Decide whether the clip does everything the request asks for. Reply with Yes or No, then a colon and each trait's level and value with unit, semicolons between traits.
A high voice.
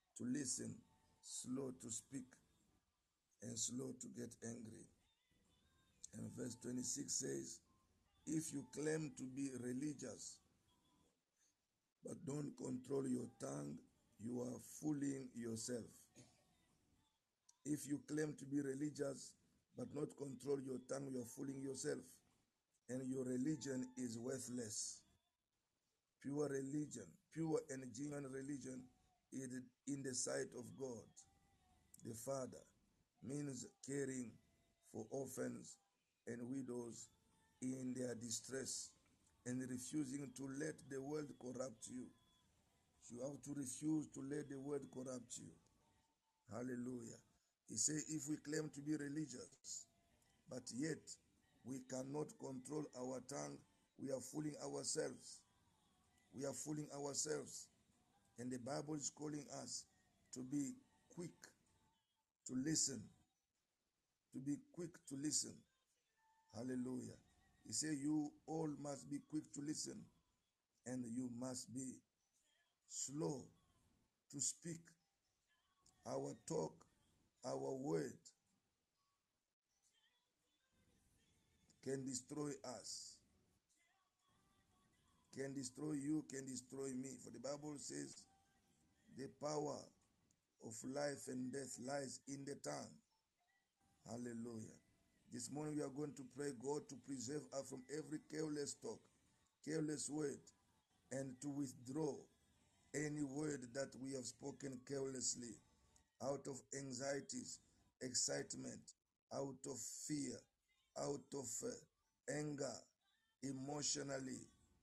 No: low, 135 Hz